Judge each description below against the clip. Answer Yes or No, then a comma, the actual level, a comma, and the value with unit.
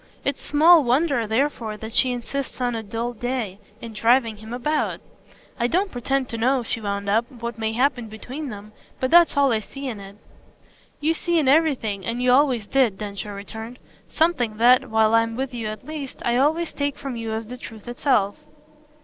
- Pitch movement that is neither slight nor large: Yes, average, 3.7 semitones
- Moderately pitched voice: No, high, 240 Hz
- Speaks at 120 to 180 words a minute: No, average, 195 wpm